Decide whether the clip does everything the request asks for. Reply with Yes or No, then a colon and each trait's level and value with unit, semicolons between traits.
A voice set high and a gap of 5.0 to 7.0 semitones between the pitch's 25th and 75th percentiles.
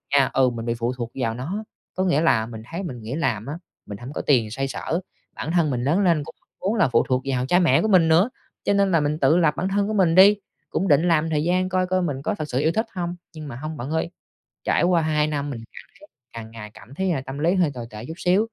No: medium, 155 Hz; wide, 5.6 semitones